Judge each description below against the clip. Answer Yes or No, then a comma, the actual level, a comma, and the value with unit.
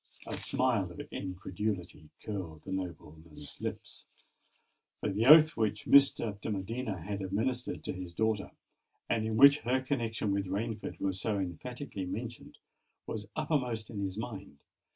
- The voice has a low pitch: Yes, low, 105 Hz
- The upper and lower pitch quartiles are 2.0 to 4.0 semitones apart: Yes, average, 3.7 semitones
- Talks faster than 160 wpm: No, average, 140 wpm